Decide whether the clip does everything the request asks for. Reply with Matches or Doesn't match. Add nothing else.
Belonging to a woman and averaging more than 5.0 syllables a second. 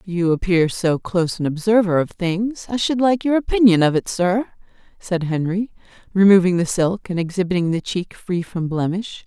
Doesn't match